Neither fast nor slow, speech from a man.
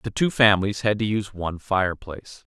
Yes: average, 190 wpm; male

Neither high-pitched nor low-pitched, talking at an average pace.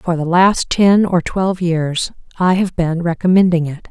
Yes: medium, 175 Hz; average, 185 wpm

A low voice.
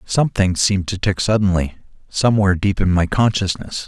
Yes: very low, 95 Hz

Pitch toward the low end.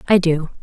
No: medium, 170 Hz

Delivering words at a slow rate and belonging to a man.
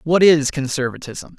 Yes: slow, 130 wpm; male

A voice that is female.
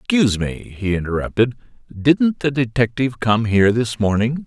No: male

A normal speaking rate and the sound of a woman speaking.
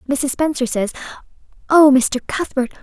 No: slow, 105 wpm; female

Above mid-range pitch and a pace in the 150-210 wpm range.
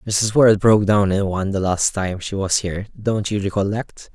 No: low, 100 Hz; fast, 205 wpm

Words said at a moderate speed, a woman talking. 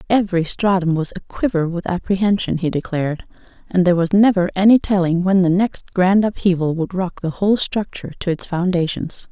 Yes: average, 175 wpm; female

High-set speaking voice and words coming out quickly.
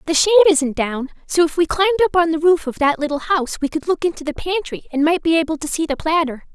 Yes: very high, 320 Hz; fast, 275 wpm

